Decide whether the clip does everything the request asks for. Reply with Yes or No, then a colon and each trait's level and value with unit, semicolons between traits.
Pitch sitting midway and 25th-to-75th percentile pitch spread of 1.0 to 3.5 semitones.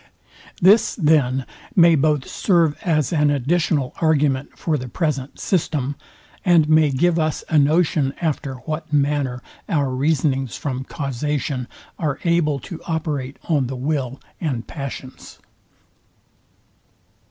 Yes: medium, 150 Hz; average, 3.1 semitones